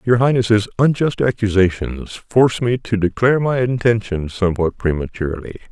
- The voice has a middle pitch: No, low, 110 Hz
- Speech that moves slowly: Yes, slow, 125 wpm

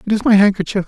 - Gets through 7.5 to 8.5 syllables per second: Yes, 8.0 syllables/s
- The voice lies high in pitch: Yes, high, 205 Hz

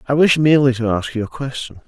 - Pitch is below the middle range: Yes, low, 130 Hz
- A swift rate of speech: Yes, fast, 255 wpm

